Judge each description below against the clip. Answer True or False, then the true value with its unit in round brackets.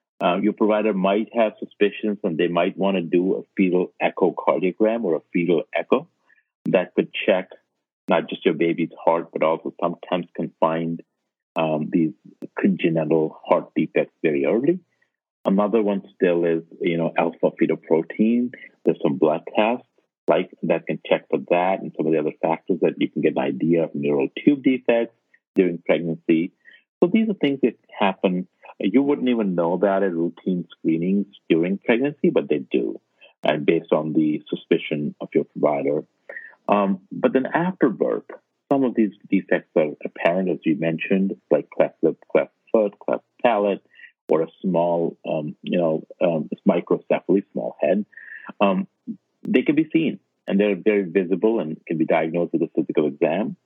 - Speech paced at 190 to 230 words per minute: False (170 wpm)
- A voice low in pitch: True (100 Hz)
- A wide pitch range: True (5.9 semitones)